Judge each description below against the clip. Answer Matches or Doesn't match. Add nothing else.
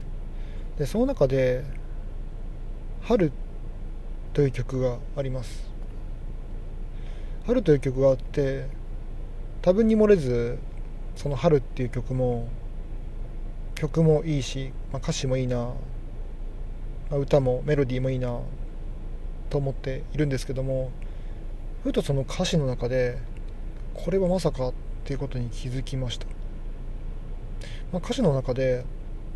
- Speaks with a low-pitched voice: Matches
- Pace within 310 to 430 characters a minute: Doesn't match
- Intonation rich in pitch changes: Doesn't match